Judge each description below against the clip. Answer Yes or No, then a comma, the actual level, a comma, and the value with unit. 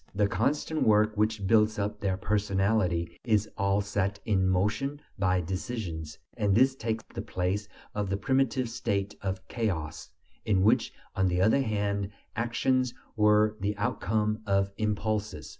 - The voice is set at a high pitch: No, low, 105 Hz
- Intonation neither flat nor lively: No, narrow, 2.1 semitones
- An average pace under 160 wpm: Yes, average, 145 wpm